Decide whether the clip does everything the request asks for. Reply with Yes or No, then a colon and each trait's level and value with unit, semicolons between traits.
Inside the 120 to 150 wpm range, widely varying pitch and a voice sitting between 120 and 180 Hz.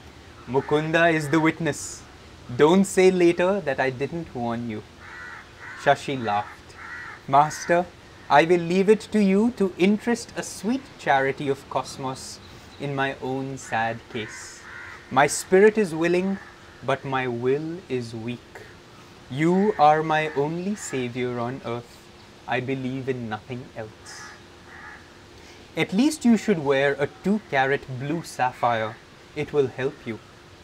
Yes: slow, 135 wpm; wide, 6.1 semitones; low, 135 Hz